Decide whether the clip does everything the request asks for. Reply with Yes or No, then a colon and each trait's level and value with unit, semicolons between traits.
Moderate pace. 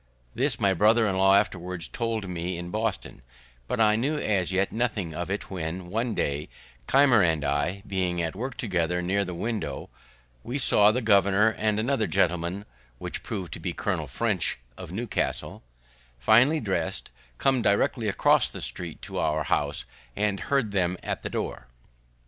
Yes: average, 165 wpm